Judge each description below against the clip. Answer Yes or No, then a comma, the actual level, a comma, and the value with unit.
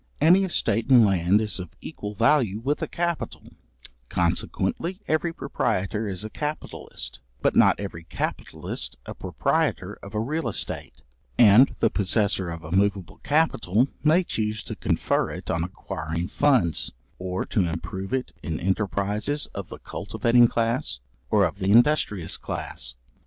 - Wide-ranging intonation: Yes, wide, 6.0 semitones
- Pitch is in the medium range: No, low, 105 Hz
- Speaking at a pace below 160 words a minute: Yes, average, 145 wpm